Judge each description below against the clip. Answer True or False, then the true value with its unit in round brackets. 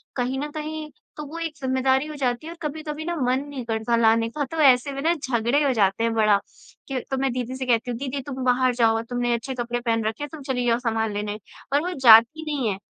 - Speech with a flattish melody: False (3.7 semitones)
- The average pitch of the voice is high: True (255 Hz)